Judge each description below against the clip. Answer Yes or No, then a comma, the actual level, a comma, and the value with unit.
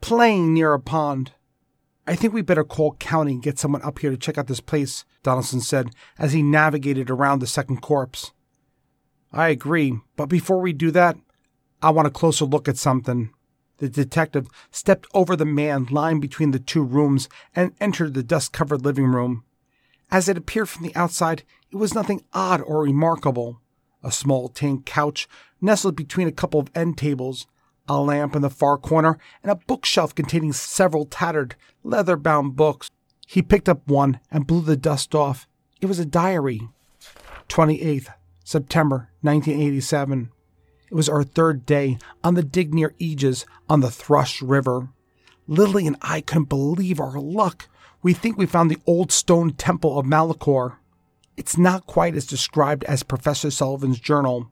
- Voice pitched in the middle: Yes, medium, 150 Hz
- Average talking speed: Yes, average, 170 wpm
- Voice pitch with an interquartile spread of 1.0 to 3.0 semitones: No, average, 3.4 semitones